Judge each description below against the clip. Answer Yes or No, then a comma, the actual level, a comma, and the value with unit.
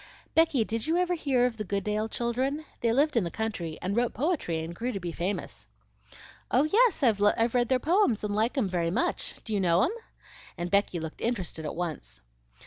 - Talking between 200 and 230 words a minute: Yes, fast, 205 wpm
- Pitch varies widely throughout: Yes, wide, 6.1 semitones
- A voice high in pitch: Yes, high, 225 Hz